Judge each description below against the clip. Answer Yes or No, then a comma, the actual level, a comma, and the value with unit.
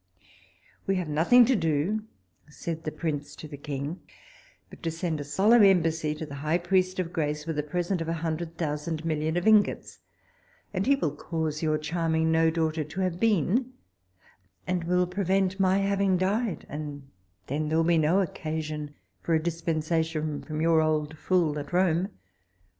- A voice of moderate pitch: Yes, medium, 165 Hz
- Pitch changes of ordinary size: Yes, average, 3.1 semitones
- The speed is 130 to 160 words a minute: No, average, 175 wpm